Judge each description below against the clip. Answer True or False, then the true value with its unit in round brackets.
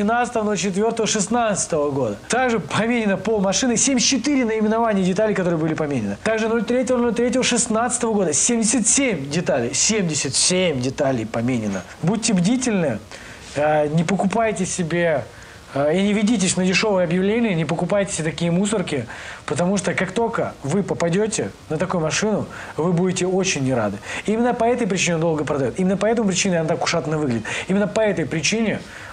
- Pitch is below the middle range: False (190 Hz)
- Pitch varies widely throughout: True (5.7 semitones)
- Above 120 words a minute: True (155 wpm)